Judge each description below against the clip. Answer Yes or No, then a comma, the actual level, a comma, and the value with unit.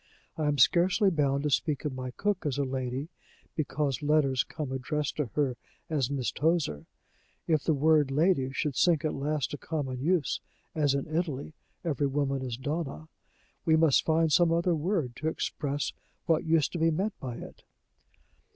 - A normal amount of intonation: Yes, average, 3.0 semitones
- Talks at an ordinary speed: Yes, average, 180 wpm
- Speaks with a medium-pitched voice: Yes, medium, 150 Hz